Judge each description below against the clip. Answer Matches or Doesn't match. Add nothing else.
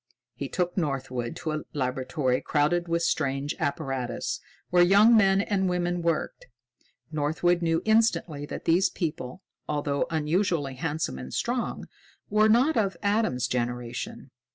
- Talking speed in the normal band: Doesn't match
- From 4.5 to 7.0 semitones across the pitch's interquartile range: Matches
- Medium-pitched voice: Matches